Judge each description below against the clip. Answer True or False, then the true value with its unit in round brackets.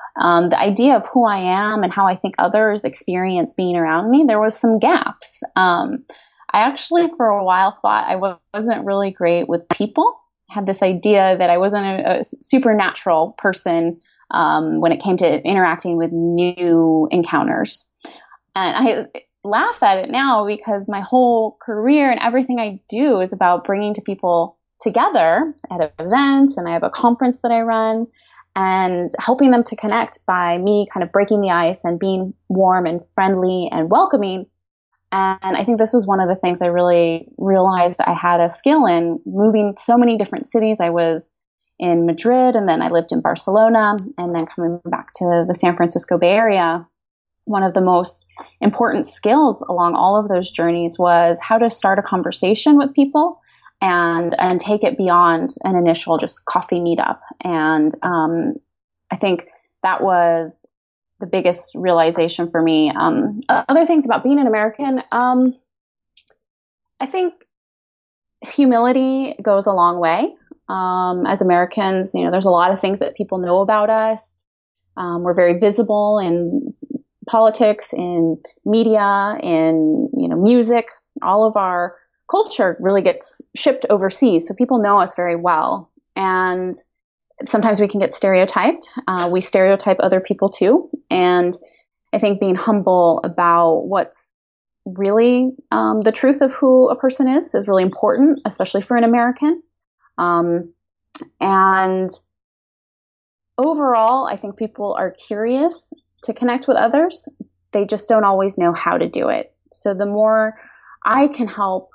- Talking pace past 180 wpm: False (160 wpm)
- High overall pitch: True (195 Hz)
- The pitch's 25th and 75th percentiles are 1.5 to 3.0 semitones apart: False (5.1 semitones)